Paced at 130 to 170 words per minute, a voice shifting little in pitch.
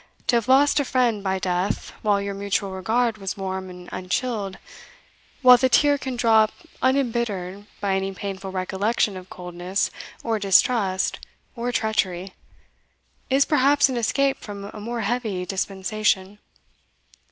No: average, 140 wpm; average, 4.0 semitones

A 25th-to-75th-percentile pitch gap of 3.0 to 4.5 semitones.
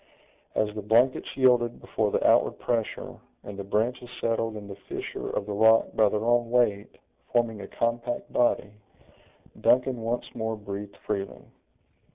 No: narrow, 2.5 semitones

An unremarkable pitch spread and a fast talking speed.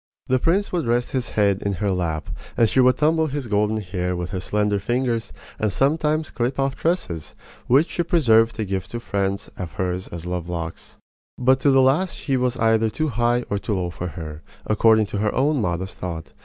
No: wide, 6.0 semitones; fast, 210 wpm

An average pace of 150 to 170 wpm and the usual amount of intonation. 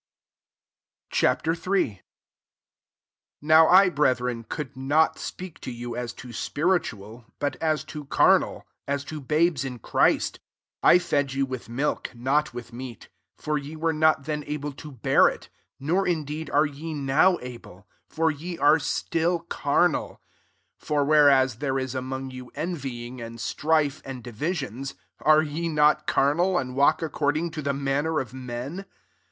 Yes: average, 160 wpm; average, 3.4 semitones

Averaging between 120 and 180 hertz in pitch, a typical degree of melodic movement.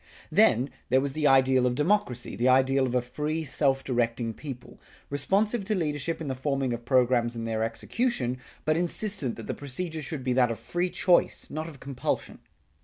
Yes: low, 135 Hz; average, 4.2 semitones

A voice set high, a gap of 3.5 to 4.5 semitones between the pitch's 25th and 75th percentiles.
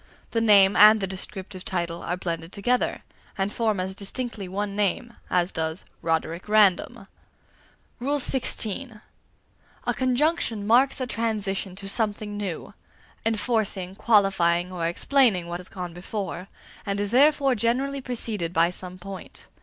Yes: high, 200 Hz; average, 4.0 semitones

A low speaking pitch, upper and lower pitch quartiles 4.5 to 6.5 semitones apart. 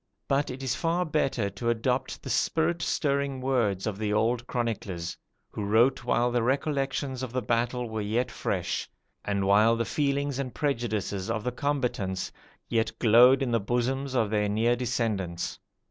No: low, 120 Hz; average, 3.7 semitones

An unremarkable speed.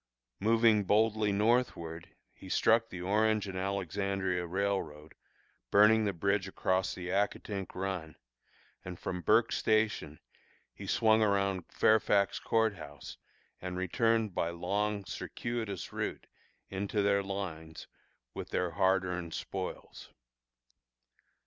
No: slow, 115 wpm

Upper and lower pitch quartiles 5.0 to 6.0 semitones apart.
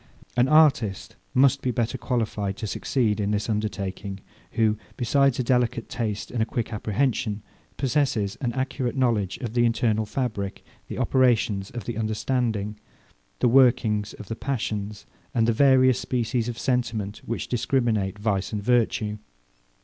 No: average, 3.1 semitones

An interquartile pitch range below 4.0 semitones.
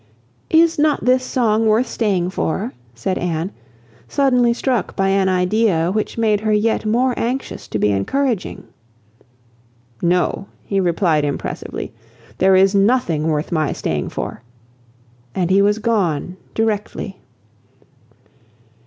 No: average, 4.4 semitones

